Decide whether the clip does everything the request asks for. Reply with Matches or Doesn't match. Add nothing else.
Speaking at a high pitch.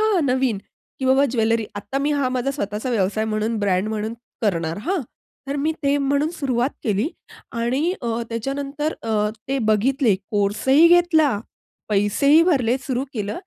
Matches